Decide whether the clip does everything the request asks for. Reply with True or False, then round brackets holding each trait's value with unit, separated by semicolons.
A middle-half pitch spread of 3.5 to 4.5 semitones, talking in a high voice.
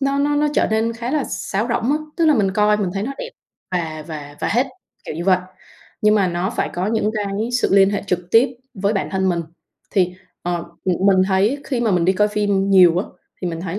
True (3.8 semitones; 200 Hz)